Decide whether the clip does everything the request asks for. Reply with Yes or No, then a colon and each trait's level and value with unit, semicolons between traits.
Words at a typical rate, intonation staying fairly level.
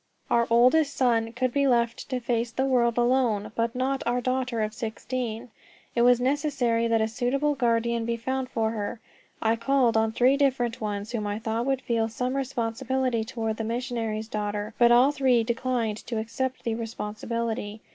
Yes: average, 175 wpm; narrow, 2.3 semitones